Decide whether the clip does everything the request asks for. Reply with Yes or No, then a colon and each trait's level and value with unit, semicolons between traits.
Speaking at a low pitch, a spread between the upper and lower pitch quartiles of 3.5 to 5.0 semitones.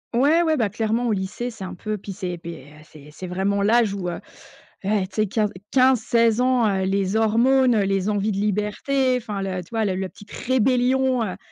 No: high, 210 Hz; average, 3.9 semitones